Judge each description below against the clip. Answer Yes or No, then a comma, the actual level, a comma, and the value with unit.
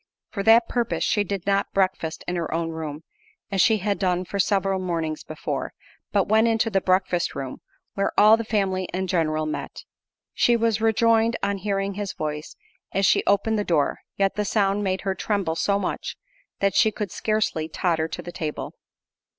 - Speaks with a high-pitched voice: Yes, high, 195 Hz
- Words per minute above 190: No, average, 185 wpm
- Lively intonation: No, average, 3.3 semitones